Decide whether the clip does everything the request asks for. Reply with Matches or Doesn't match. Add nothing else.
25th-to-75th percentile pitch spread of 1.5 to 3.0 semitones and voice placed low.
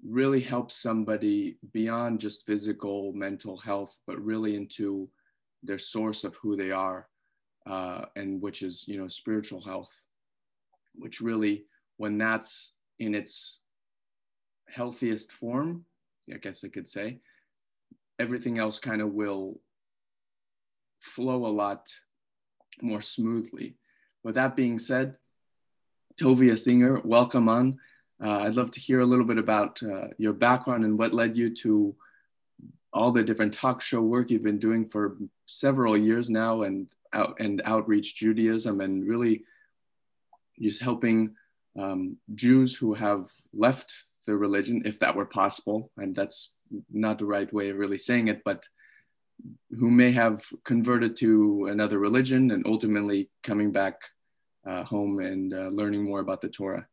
Matches